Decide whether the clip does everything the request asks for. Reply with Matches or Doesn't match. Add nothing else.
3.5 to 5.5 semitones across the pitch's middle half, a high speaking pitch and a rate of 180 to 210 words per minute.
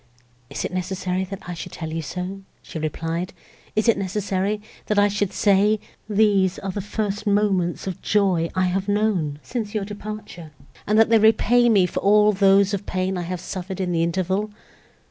Doesn't match